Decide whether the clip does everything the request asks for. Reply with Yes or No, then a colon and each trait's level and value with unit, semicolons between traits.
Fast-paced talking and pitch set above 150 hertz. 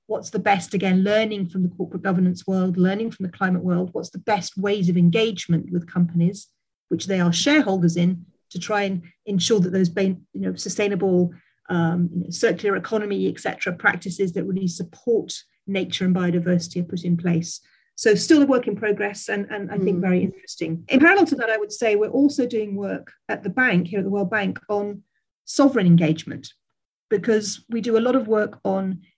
No: average, 195 wpm; high, 190 Hz